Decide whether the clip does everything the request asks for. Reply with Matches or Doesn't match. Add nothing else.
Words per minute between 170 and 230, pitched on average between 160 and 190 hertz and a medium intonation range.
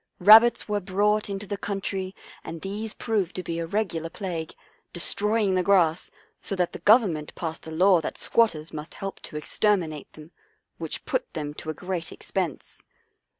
Matches